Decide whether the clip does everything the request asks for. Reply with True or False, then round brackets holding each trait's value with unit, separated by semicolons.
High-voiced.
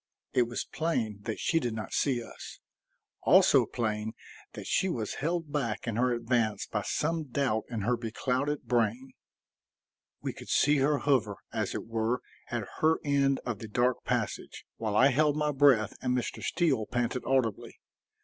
False (125 Hz)